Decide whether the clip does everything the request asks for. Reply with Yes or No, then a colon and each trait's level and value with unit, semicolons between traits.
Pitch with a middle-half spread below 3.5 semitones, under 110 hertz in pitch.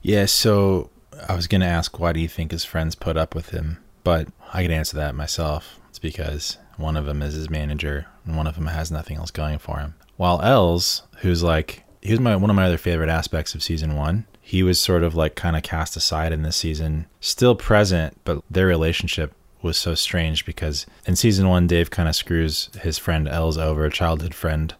Yes: narrow, 2.4 semitones; very low, 80 Hz